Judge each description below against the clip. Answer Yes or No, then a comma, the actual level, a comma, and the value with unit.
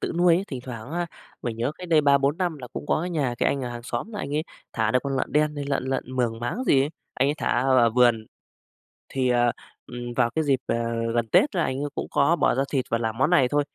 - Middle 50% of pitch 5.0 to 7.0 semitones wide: No, average, 3.9 semitones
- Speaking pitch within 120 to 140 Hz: Yes, low, 135 Hz